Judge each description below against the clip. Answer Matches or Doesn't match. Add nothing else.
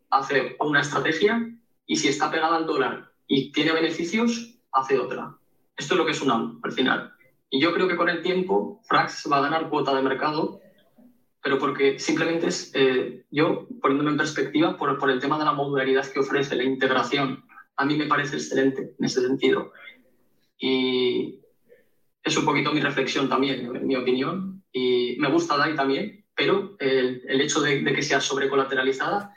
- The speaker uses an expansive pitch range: Matches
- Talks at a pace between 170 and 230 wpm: Matches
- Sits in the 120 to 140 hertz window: Doesn't match